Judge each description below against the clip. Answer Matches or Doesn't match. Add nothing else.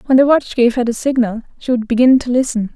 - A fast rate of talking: Matches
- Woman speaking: Matches